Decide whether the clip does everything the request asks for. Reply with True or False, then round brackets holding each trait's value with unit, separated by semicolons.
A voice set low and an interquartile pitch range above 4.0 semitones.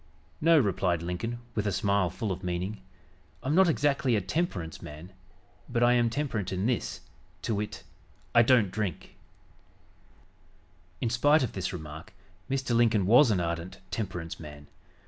True (105 Hz; 5.2 semitones)